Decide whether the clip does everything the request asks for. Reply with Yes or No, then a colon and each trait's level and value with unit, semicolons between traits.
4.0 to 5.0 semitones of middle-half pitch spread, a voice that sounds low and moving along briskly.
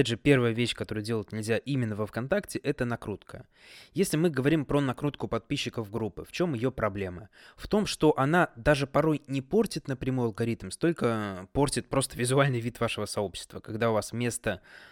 Yes: average, 4.4 semitones; low, 120 Hz; fast, 175 wpm